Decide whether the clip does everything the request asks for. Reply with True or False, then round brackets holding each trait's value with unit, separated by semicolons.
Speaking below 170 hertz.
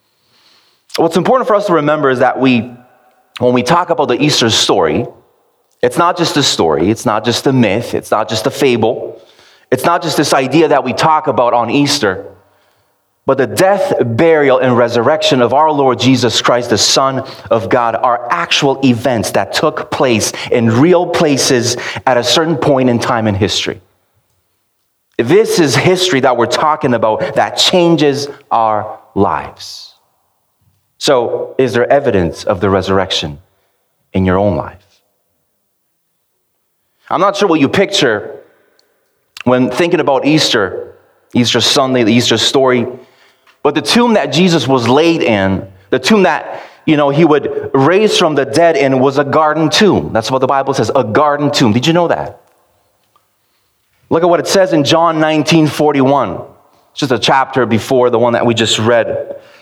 True (135 Hz)